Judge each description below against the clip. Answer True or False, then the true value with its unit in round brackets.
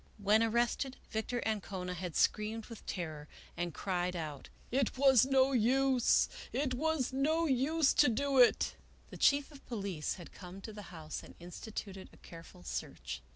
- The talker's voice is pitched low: False (225 Hz)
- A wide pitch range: True (6.7 semitones)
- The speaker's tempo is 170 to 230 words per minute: True (175 wpm)